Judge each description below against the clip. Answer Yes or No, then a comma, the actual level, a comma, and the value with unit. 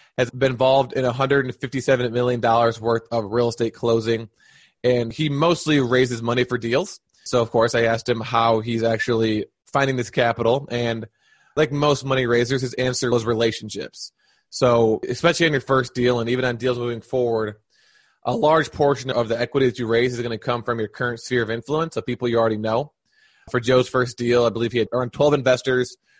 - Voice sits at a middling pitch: No, low, 120 Hz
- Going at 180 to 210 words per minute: Yes, average, 200 wpm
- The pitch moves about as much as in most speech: No, narrow, 2.2 semitones